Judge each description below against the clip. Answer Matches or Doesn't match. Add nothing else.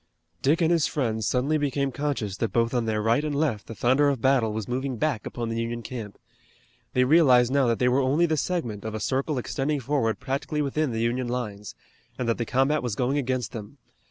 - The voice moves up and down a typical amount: Matches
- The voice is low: Matches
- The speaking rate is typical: Doesn't match